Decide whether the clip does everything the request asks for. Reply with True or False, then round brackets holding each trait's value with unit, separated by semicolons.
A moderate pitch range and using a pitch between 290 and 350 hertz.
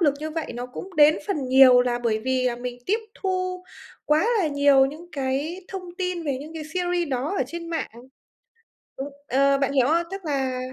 True (4.8 semitones; 295 Hz)